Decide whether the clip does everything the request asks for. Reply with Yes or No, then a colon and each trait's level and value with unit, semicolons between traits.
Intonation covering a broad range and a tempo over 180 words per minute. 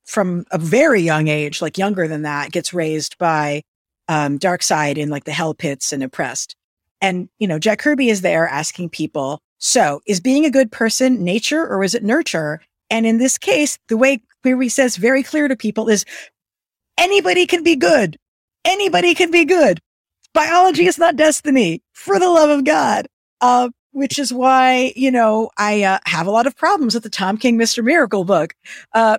Yes: wide, 8.3 semitones; average, 190 wpm